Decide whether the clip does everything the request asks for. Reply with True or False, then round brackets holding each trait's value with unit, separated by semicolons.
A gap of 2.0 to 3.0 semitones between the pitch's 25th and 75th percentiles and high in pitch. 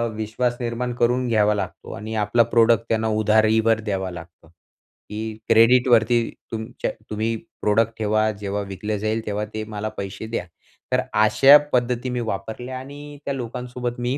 False (2.5 semitones; 110 Hz)